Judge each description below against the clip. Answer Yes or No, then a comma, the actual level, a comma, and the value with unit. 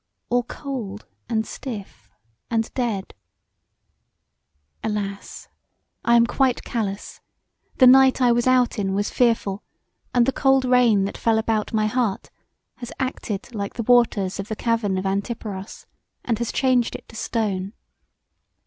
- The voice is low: No, high, 225 Hz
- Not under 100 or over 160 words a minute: Yes, average, 140 wpm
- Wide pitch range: No, average, 3.5 semitones